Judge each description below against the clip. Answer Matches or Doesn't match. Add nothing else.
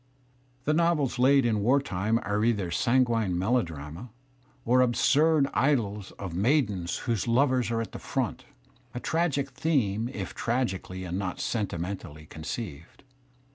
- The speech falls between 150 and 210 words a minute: Doesn't match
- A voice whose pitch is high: Doesn't match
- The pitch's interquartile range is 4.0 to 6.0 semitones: Matches